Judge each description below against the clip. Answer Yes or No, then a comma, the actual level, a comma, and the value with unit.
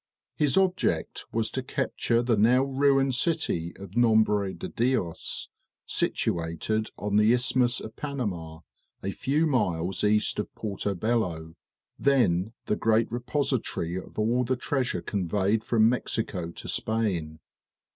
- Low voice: Yes, low, 110 Hz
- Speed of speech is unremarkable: No, slow, 130 wpm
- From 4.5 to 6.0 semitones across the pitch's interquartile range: Yes, average, 4.8 semitones